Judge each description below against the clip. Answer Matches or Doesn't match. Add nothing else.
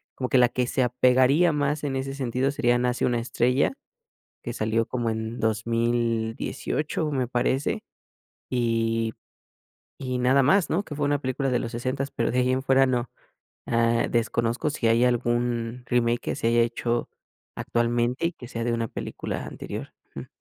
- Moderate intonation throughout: Doesn't match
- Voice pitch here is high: Doesn't match